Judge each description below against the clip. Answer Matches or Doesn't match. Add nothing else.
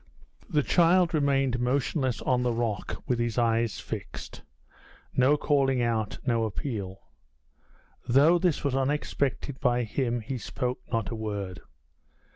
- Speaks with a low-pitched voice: Matches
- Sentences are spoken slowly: Matches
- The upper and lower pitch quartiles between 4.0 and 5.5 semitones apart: Doesn't match